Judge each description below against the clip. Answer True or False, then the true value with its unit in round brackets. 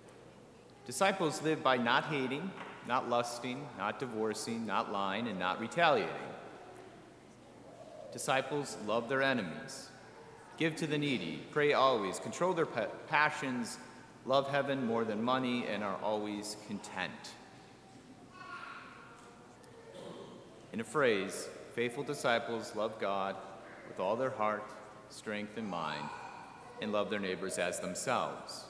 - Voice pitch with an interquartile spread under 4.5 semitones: False (4.9 semitones)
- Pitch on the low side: True (120 Hz)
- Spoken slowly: True (115 wpm)